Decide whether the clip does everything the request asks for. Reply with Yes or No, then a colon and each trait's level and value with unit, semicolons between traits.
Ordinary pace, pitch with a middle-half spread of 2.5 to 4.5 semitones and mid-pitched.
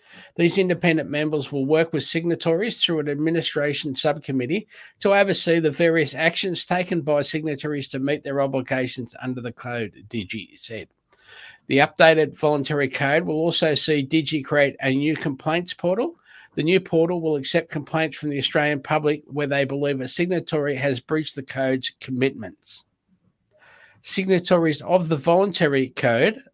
Yes: average, 150 wpm; average, 3.1 semitones; medium, 155 Hz